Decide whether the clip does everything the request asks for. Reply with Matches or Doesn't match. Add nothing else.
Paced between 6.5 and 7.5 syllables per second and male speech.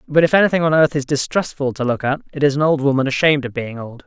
Matches